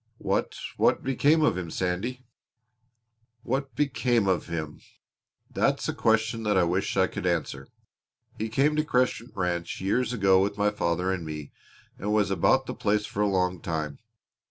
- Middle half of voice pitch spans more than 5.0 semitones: Yes, wide, 5.5 semitones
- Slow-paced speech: No, average, 165 wpm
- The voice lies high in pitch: No, low, 100 Hz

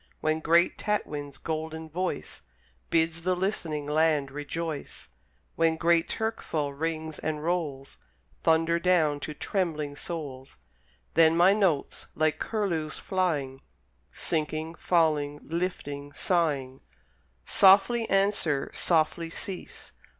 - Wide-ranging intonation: No, average, 2.8 semitones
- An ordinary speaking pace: No, slow, 105 wpm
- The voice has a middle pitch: Yes, medium, 160 Hz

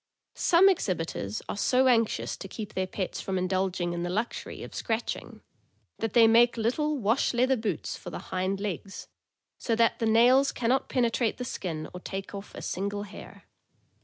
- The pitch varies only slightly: No, average, 4.2 semitones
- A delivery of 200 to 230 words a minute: No, average, 185 wpm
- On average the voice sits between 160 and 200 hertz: No, high, 220 Hz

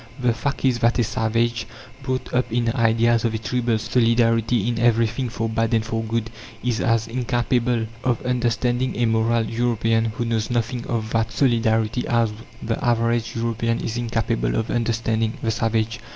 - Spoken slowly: No, average, 165 wpm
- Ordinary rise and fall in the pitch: No, narrow, 1.1 semitones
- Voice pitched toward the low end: Yes, low, 115 Hz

